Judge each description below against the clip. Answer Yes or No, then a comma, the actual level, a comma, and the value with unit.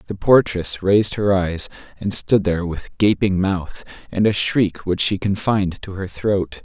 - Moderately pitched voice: No, very low, 95 Hz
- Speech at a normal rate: Yes, average, 180 wpm